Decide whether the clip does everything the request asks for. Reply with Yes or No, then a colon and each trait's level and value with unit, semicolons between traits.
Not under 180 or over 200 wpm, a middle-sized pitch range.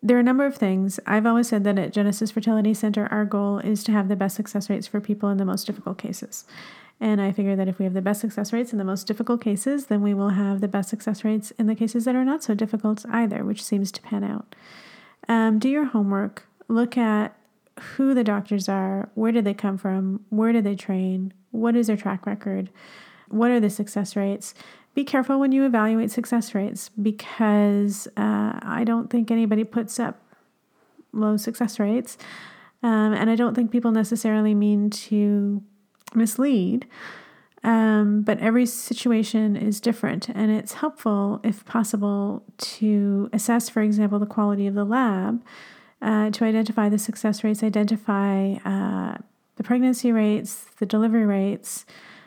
No: average, 185 wpm; narrow, 2.1 semitones